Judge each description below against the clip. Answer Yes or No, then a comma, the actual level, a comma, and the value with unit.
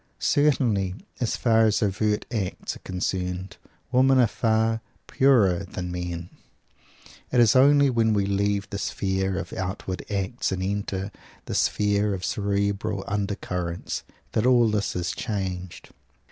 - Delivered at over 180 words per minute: No, slow, 135 wpm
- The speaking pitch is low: Yes, low, 100 Hz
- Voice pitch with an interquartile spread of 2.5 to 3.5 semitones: Yes, average, 2.9 semitones